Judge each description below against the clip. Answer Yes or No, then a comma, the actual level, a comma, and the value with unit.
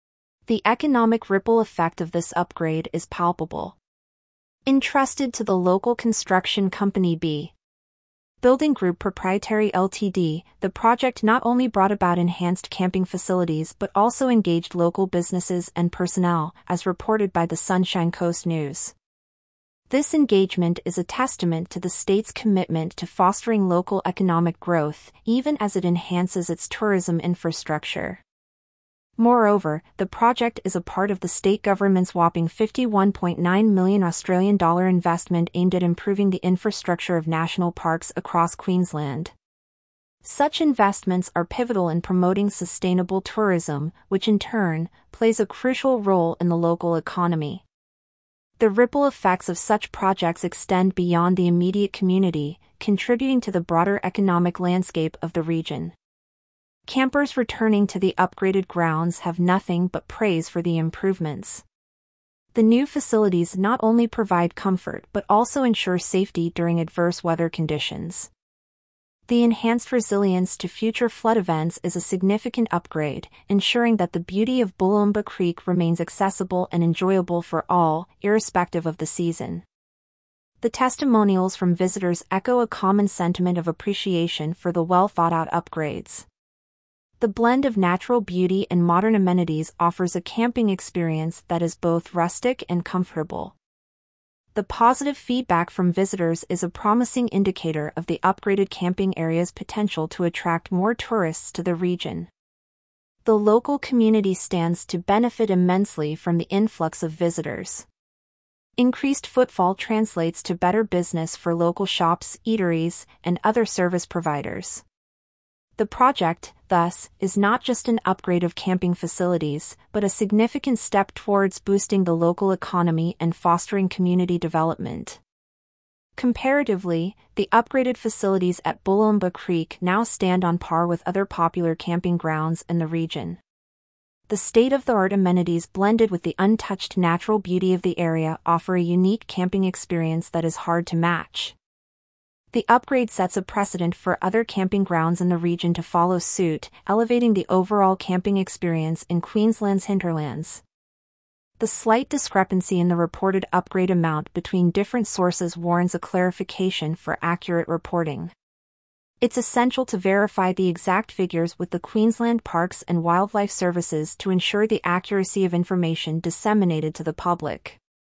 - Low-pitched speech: No, medium, 185 Hz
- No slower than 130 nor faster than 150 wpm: Yes, average, 140 wpm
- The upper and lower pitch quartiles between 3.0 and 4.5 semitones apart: Yes, average, 3.3 semitones